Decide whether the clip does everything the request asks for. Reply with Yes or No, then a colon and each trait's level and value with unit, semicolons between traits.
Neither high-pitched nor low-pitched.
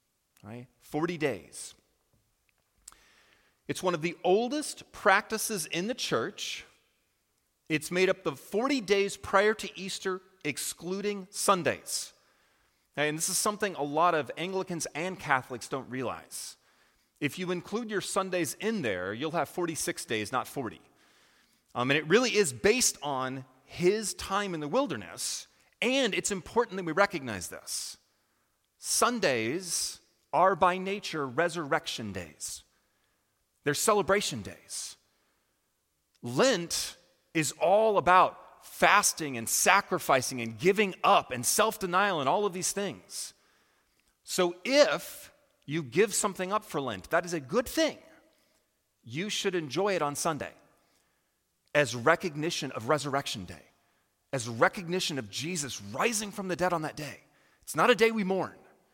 Yes: medium, 175 Hz